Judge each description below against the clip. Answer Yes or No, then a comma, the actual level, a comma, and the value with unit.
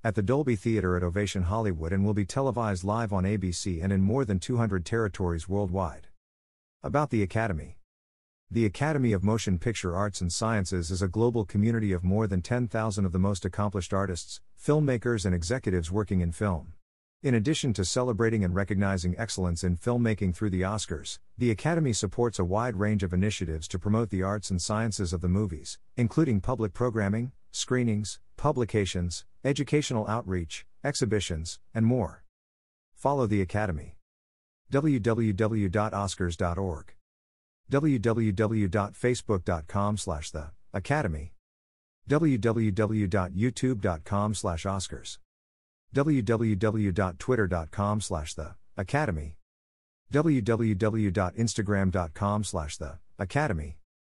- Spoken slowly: Yes, slow, 120 wpm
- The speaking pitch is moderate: No, low, 100 Hz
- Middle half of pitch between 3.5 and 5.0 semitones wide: Yes, average, 4.2 semitones